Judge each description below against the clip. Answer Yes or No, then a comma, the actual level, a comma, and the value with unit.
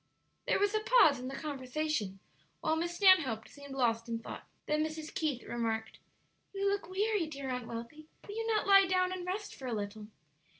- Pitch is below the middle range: No, very high, 305 Hz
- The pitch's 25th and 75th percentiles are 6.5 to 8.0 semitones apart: Yes, wide, 7.7 semitones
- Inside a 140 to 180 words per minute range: No, average, 195 wpm